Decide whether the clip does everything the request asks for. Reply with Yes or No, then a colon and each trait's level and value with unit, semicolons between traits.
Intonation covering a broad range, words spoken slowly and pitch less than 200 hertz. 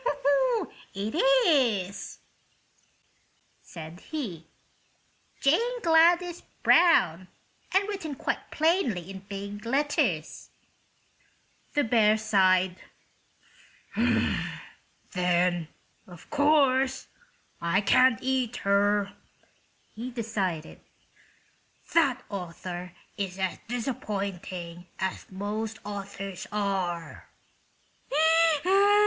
No: wide, 6.1 semitones; slow, 70 wpm; high, 205 Hz